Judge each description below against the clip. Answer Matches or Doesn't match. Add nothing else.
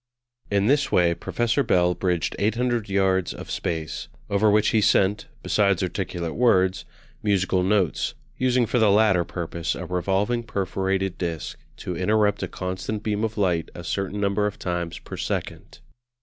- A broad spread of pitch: Doesn't match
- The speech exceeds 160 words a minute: Doesn't match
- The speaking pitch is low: Matches